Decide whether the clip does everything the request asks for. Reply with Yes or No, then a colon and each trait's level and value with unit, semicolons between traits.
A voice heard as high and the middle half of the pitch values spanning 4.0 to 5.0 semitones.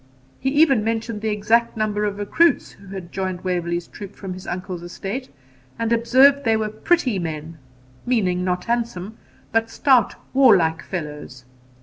Yes: high, 210 Hz; average, 4.4 semitones